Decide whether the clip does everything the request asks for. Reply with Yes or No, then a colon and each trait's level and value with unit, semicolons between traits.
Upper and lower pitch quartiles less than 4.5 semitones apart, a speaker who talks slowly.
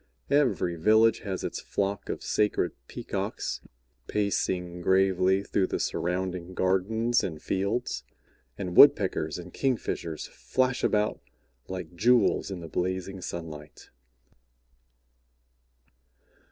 Yes: average, 3.1 semitones; slow, 100 wpm